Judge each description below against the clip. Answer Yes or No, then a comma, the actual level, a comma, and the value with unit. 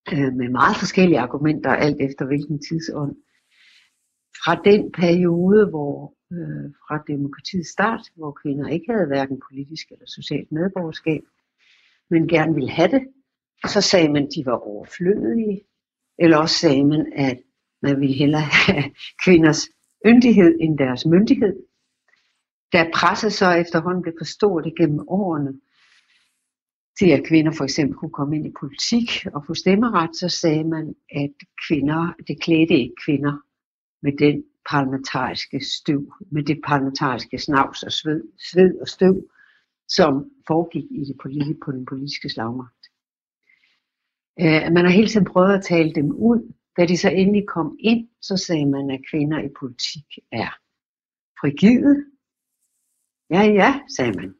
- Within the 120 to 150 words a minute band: Yes, slow, 145 wpm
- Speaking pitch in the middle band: Yes, medium, 160 Hz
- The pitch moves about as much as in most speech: Yes, average, 4.5 semitones